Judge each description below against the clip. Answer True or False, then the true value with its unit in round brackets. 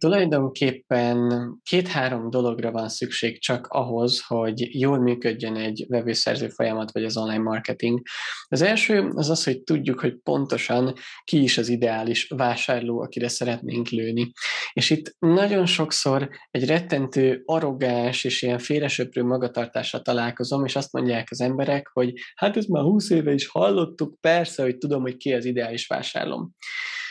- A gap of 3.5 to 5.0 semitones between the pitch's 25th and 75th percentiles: True (3.8 semitones)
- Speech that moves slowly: False (145 wpm)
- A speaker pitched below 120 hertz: False (125 Hz)